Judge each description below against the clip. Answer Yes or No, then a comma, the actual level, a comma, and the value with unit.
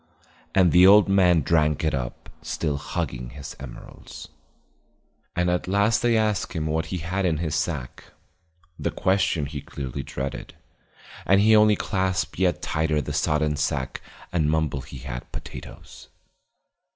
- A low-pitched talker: Yes, very low, 80 Hz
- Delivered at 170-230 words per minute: No, average, 150 wpm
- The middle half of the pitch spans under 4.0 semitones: No, average, 4.4 semitones